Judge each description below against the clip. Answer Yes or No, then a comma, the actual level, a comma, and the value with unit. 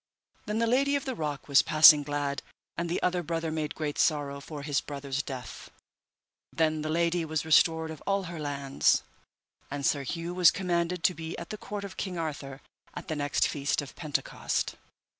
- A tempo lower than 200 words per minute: Yes, average, 190 wpm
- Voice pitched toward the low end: No, medium, 160 Hz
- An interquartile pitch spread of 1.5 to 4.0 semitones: Yes, average, 3.1 semitones